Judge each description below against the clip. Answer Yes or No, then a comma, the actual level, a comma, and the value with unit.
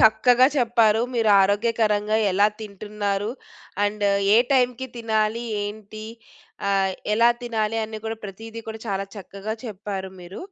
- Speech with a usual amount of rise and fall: No, narrow, 1.9 semitones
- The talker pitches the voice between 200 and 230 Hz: Yes, high, 215 Hz